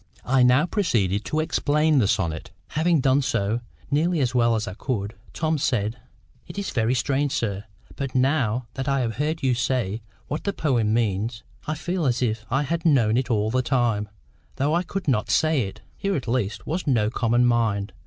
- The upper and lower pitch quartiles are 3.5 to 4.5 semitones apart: No, average, 5.0 semitones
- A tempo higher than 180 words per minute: Yes, average, 195 wpm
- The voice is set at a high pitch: No, low, 125 Hz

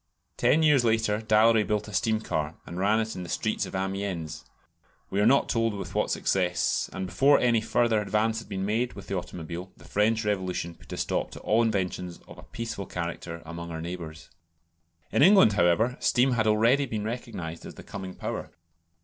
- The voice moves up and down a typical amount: Yes, average, 4.1 semitones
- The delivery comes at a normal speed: Yes, average, 195 wpm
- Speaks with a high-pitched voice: No, low, 105 Hz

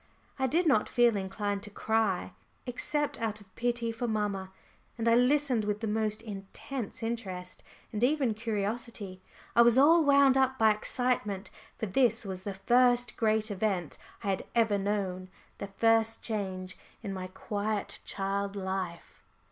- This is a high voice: Yes, high, 215 Hz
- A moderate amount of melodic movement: Yes, average, 3.4 semitones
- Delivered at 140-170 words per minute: Yes, average, 155 wpm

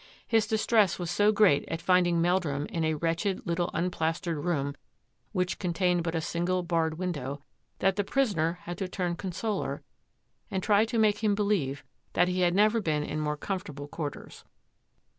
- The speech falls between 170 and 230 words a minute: Yes, average, 175 wpm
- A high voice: No, medium, 175 Hz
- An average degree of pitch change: Yes, average, 3.5 semitones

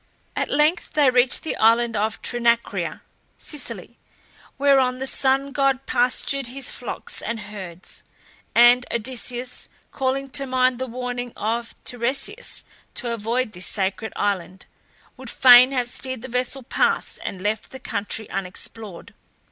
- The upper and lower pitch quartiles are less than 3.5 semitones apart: Yes, average, 2.9 semitones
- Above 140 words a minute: No, slow, 135 wpm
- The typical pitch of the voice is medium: No, high, 245 Hz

